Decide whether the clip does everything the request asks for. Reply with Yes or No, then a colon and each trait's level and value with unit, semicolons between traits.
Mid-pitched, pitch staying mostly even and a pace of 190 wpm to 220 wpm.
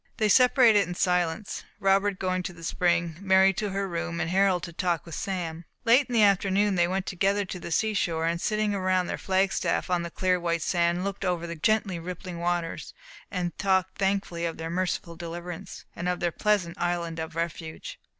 Yes: medium, 180 Hz; narrow, 2.3 semitones; average, 200 wpm